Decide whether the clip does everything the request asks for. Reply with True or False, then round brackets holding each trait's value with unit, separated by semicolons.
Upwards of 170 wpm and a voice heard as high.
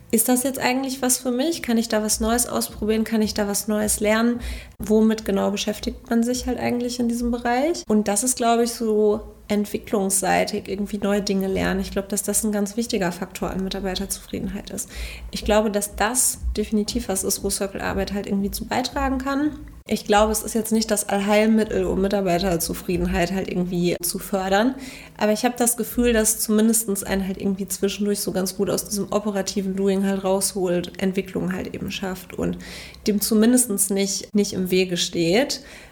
True (185 wpm; 210 Hz)